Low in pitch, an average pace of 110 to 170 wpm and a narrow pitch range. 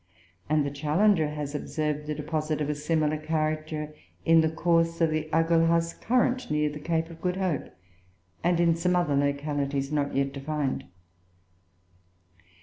No: medium, 155 Hz; average, 150 wpm; narrow, 2.0 semitones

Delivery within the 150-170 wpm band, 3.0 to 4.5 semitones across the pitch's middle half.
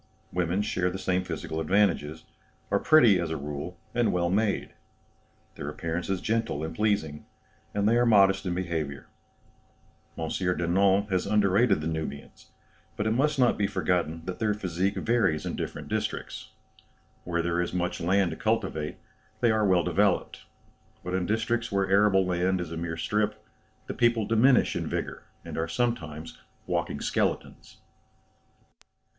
Yes: average, 155 wpm; average, 4.0 semitones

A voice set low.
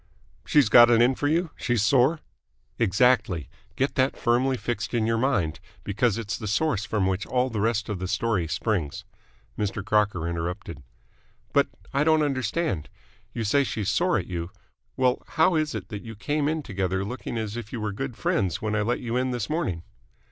Yes: low, 115 Hz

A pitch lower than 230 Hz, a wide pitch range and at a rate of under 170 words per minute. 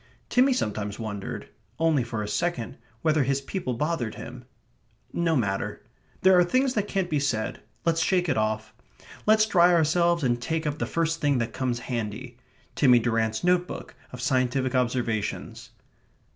Yes: low, 135 Hz; wide, 6.4 semitones; average, 160 wpm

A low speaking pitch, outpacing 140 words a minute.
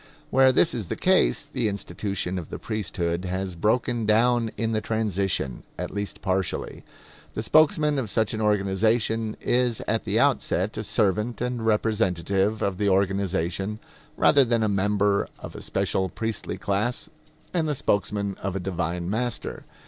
Yes: low, 105 Hz; average, 155 wpm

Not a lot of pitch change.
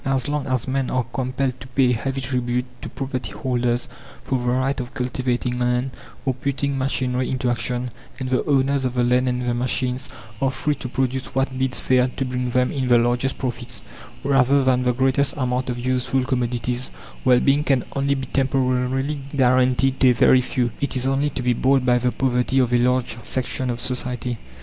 Yes: narrow, 1.3 semitones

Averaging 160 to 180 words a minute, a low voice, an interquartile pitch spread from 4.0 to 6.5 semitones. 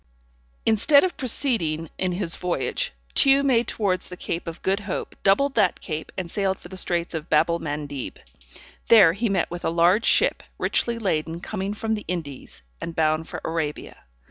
No: average, 175 wpm; medium, 180 Hz; average, 4.5 semitones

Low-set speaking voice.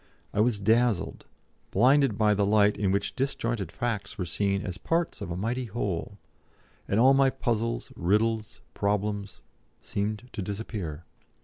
Yes: low, 105 Hz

